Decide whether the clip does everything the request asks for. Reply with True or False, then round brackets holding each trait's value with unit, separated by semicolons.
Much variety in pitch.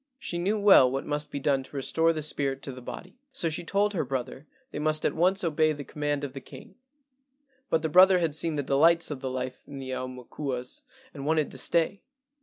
False (3.7 semitones)